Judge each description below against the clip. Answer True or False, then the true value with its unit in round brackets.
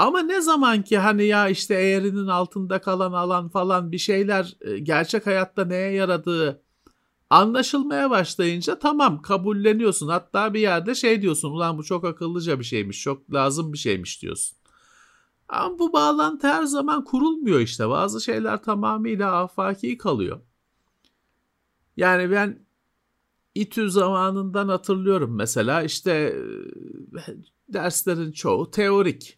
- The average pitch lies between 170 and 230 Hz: True (190 Hz)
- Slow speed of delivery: False (125 wpm)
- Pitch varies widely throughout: False (4.4 semitones)